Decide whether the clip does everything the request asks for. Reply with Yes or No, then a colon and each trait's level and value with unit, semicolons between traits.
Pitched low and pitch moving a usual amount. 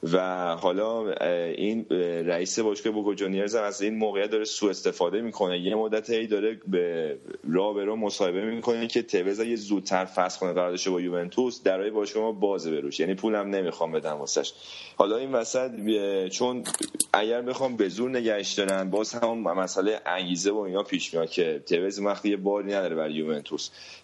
Yes: low, 105 Hz; average, 3.8 semitones